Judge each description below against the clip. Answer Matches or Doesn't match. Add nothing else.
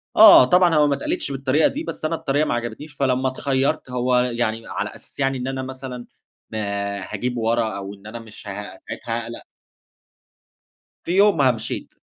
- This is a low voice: Matches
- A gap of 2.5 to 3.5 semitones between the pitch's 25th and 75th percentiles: Matches